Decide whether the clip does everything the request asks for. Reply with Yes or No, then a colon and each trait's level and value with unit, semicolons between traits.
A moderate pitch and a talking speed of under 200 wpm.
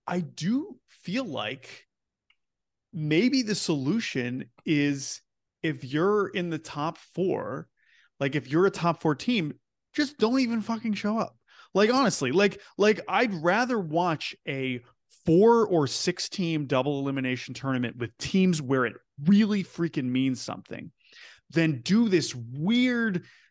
Yes: medium, 170 Hz; average, 140 wpm